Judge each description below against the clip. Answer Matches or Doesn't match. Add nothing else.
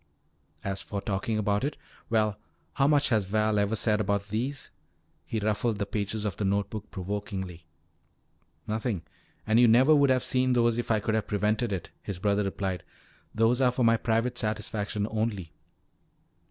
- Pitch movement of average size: Doesn't match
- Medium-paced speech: Matches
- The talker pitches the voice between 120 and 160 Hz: Doesn't match